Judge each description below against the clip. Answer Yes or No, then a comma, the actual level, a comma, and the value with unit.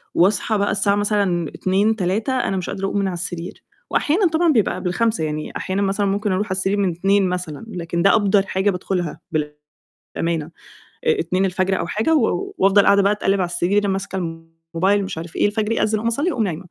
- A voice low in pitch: No, high, 195 Hz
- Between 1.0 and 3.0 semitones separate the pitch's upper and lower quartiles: Yes, narrow, 2.5 semitones